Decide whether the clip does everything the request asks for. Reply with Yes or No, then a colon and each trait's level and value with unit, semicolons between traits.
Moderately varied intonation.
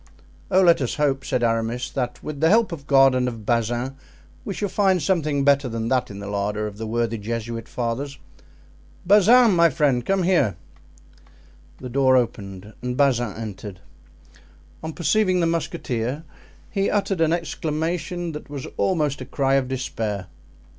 No: wide, 6.2 semitones